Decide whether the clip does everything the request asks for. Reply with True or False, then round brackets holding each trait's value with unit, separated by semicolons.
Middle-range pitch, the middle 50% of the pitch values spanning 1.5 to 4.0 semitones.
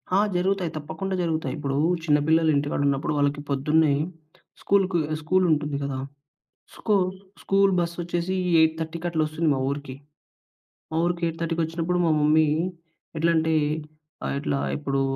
True (160 Hz; 2.8 semitones)